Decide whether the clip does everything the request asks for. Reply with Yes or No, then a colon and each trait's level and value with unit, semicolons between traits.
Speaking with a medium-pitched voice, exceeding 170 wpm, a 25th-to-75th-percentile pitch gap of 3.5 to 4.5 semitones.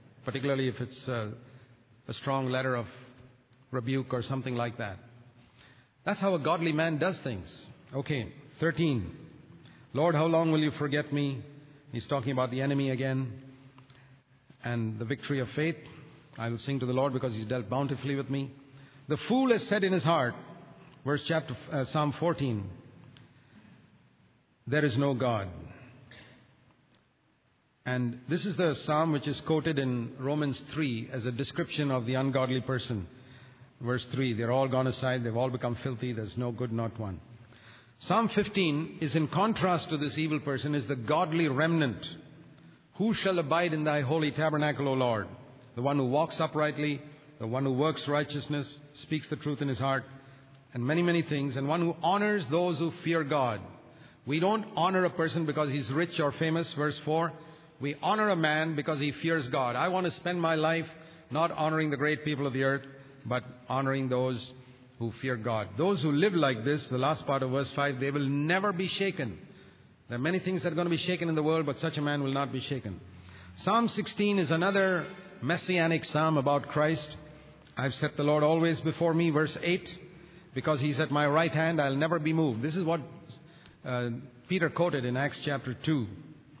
Yes: medium, 145 Hz; average, 185 wpm; average, 4.0 semitones